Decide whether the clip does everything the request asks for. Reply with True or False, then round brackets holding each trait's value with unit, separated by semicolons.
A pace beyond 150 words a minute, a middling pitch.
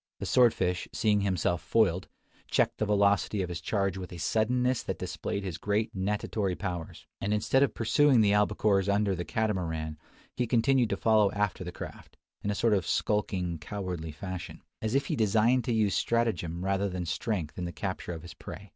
False (190 wpm; 100 Hz)